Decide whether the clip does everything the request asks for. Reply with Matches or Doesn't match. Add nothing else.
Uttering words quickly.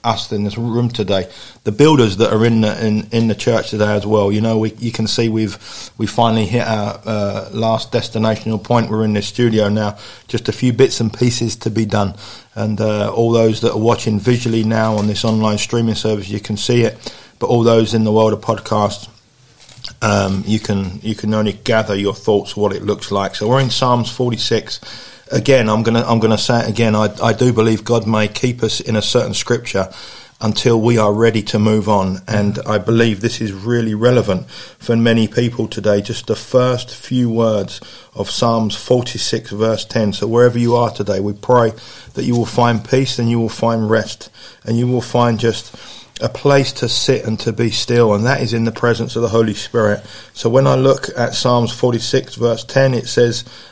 Matches